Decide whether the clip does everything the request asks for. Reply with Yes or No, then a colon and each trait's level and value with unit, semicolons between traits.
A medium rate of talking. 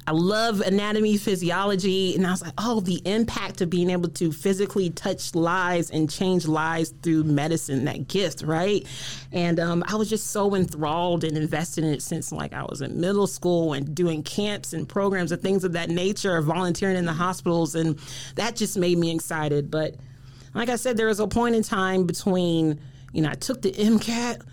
Yes: average, 190 wpm